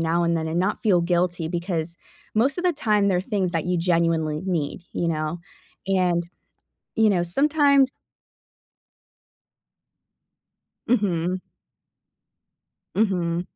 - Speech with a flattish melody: No, average, 3.4 semitones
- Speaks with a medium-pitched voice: Yes, medium, 180 Hz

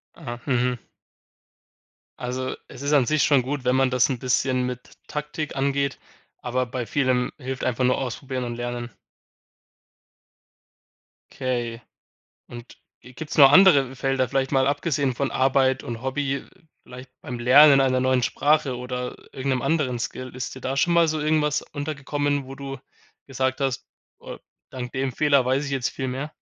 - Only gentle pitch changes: Yes, narrow, 2.0 semitones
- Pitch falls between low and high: No, low, 130 Hz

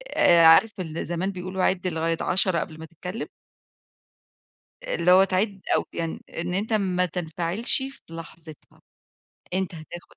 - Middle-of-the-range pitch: Yes, medium, 180 Hz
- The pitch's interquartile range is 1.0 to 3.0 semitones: Yes, narrow, 2.5 semitones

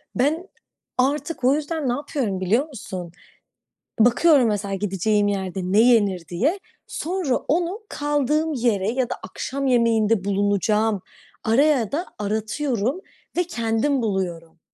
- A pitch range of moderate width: No, wide, 6.3 semitones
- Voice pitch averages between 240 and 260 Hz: No, high, 230 Hz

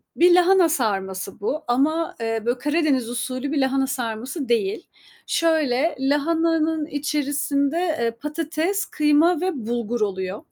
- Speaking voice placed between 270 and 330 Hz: Yes, very high, 280 Hz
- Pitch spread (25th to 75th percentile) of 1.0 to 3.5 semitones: No, average, 5.1 semitones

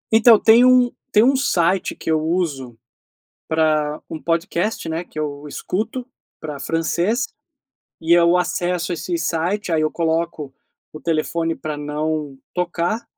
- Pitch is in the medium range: Yes, medium, 165 Hz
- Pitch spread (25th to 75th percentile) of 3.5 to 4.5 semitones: No, average, 3.1 semitones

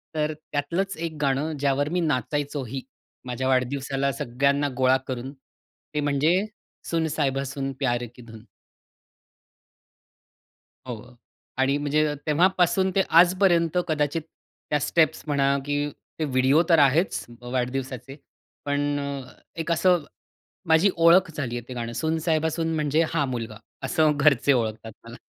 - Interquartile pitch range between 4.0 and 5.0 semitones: No, average, 3.4 semitones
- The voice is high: No, medium, 145 Hz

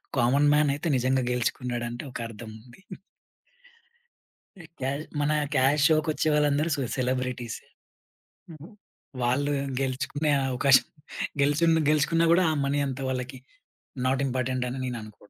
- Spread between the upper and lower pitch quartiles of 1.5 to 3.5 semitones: Yes, average, 2.9 semitones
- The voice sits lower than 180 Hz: Yes, low, 135 Hz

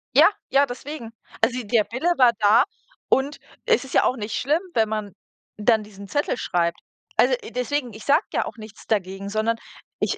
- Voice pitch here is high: Yes, high, 230 Hz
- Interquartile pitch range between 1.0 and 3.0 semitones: No, average, 4.2 semitones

